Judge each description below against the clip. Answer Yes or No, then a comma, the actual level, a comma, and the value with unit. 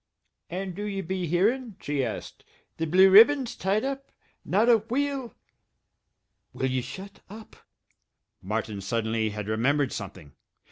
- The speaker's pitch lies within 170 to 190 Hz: Yes, medium, 185 Hz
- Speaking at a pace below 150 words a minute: Yes, average, 140 wpm